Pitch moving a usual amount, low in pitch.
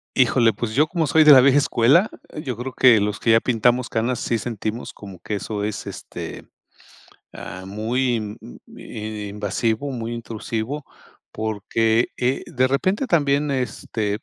Yes: average, 3.5 semitones; low, 115 Hz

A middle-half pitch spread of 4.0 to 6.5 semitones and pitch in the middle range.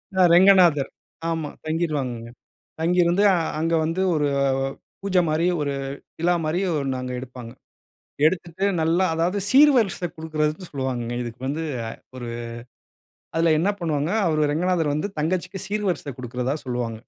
Yes: average, 4.4 semitones; medium, 160 Hz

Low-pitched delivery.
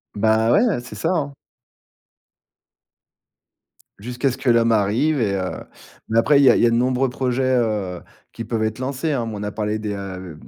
Yes: low, 115 Hz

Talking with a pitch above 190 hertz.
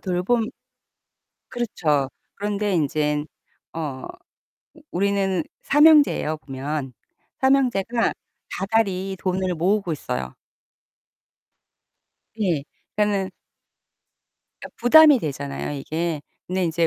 No: medium, 185 Hz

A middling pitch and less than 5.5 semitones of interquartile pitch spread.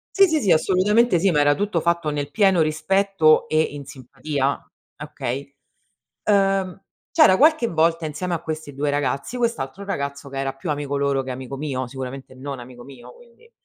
No: medium, 155 Hz; wide, 5.8 semitones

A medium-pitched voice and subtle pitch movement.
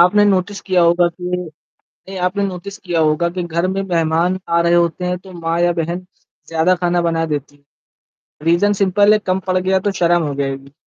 Yes: medium, 175 Hz; narrow, 1.9 semitones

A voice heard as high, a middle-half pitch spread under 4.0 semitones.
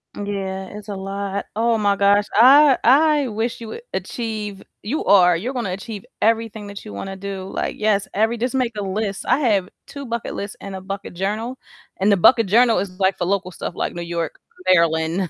Yes: high, 205 Hz; average, 3.1 semitones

